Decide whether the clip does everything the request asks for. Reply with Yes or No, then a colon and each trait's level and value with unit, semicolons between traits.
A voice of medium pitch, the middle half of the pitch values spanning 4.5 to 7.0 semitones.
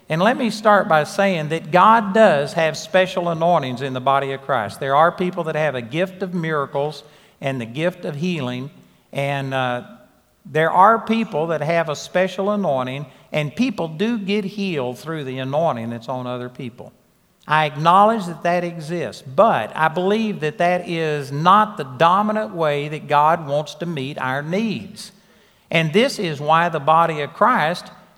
Yes: medium, 165 Hz; average, 5.1 semitones